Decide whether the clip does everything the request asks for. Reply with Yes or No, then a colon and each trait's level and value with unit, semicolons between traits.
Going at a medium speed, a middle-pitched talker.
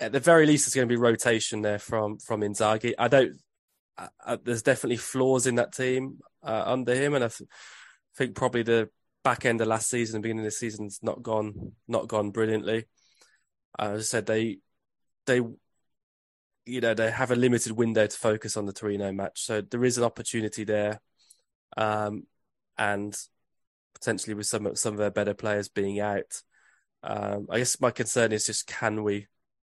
No: average, 185 wpm; low, 110 Hz